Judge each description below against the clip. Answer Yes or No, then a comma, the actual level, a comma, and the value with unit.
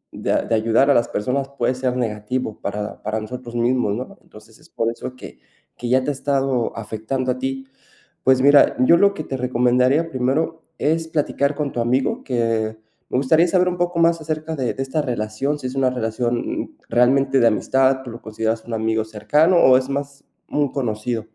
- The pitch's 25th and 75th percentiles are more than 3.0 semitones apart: Yes, average, 3.4 semitones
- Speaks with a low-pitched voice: Yes, low, 130 Hz